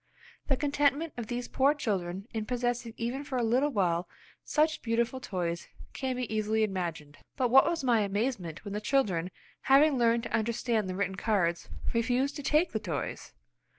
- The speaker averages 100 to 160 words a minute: No, average, 175 wpm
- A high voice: Yes, high, 230 Hz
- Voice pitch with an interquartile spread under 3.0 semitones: No, average, 5.1 semitones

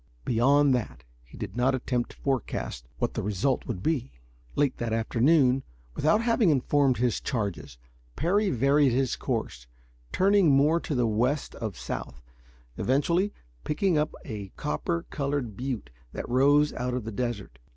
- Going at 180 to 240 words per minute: No, average, 150 wpm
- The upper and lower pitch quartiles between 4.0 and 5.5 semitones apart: Yes, average, 4.5 semitones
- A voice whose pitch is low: Yes, low, 130 Hz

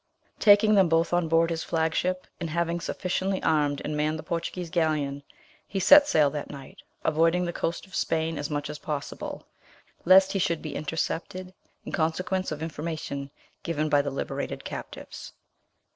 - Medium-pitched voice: Yes, medium, 165 Hz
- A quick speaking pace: No, average, 170 wpm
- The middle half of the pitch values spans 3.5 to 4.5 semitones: No, average, 2.9 semitones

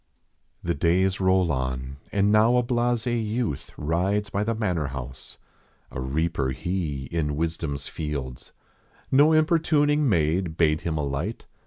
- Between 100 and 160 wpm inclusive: Yes, average, 140 wpm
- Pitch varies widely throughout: Yes, wide, 7.1 semitones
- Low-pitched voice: Yes, very low, 85 Hz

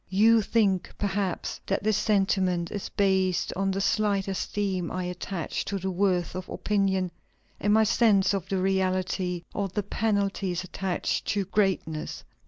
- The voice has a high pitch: Yes, high, 195 Hz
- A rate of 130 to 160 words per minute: Yes, average, 150 wpm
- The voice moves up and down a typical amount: No, narrow, 1.7 semitones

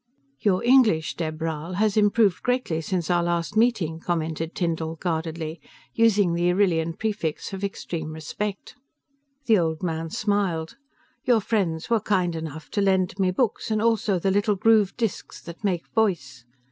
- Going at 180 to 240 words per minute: No, average, 155 wpm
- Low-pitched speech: No, medium, 180 Hz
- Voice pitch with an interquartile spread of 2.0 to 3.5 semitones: No, average, 4.3 semitones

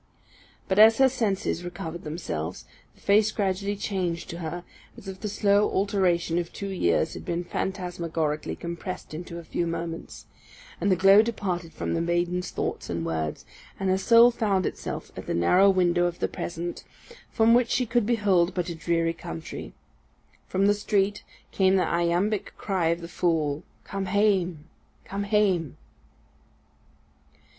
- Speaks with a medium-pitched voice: Yes, medium, 180 Hz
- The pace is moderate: Yes, average, 160 wpm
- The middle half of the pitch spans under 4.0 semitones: Yes, average, 3.0 semitones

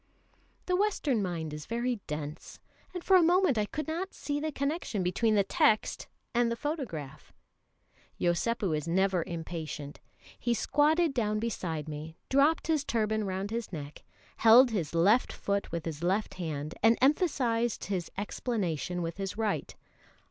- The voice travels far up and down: Yes, wide, 7.7 semitones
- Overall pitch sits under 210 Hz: No, high, 215 Hz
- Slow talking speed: No, average, 155 wpm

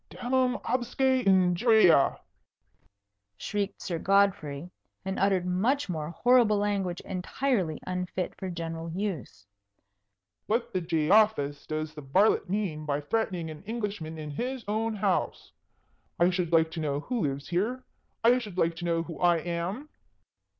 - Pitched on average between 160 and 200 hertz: Yes, medium, 185 Hz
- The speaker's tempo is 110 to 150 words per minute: Yes, average, 140 wpm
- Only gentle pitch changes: No, average, 4.9 semitones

